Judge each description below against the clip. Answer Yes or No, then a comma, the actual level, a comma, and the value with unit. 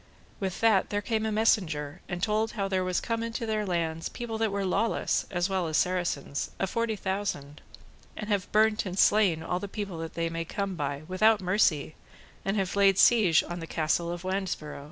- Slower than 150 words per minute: No, average, 200 wpm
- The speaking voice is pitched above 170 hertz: Yes, high, 190 Hz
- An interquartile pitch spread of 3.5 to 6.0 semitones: Yes, average, 3.9 semitones